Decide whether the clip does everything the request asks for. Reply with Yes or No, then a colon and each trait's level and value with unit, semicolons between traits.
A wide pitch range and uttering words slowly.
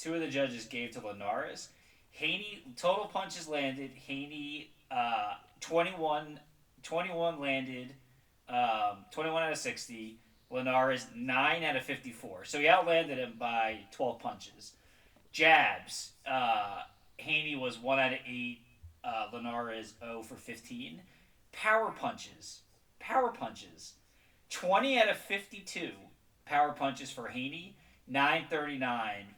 No: average, 4.9 semitones; slow, 125 wpm